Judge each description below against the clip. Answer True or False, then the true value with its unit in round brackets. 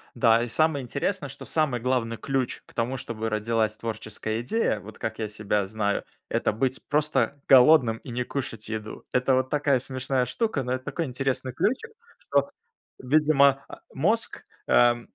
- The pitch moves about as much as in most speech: True (3.6 semitones)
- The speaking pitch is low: True (125 Hz)